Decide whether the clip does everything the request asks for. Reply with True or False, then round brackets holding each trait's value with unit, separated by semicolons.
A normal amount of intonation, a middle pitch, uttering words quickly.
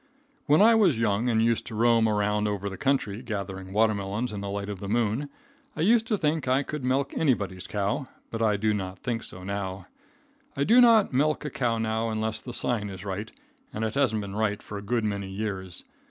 False (4.1 semitones; 110 Hz; 220 wpm)